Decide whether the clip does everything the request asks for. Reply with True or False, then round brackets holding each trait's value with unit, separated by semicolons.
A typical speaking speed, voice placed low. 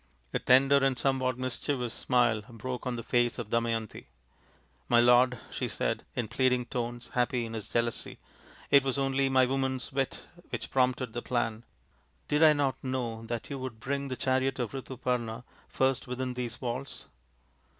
True (175 wpm; 125 Hz)